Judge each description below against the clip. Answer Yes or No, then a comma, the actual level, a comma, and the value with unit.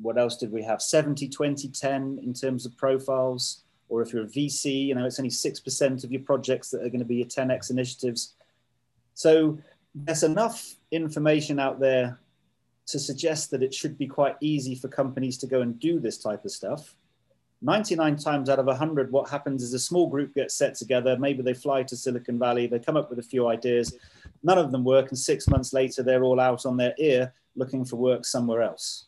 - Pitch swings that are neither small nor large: No, narrow, 2.2 semitones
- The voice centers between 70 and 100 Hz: No, low, 130 Hz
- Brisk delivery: Yes, fast, 215 wpm